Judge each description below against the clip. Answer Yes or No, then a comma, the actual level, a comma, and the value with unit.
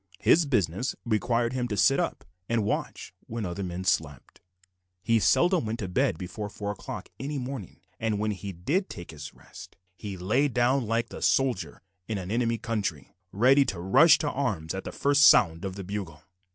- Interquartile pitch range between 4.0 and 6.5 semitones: Yes, average, 5.3 semitones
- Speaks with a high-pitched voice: No, low, 110 Hz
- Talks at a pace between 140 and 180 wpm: No, average, 190 wpm